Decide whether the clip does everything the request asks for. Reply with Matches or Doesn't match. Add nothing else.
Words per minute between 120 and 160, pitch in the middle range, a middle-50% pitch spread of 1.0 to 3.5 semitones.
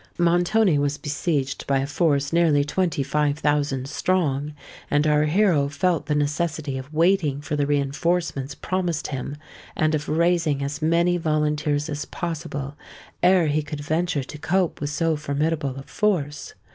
Matches